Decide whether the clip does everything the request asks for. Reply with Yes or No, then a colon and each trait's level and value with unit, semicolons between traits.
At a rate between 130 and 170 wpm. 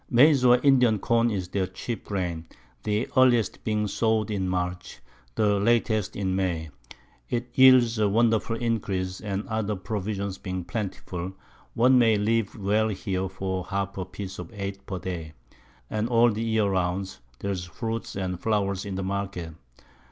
Yes: average, 160 wpm